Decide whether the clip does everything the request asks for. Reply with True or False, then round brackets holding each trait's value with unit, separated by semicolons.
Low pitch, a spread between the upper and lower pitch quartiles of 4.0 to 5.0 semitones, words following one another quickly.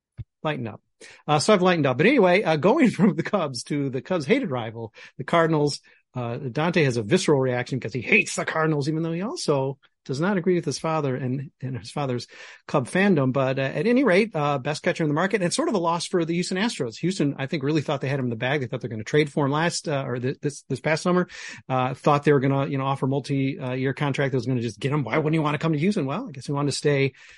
False (150 Hz; 4.3 semitones; 285 wpm)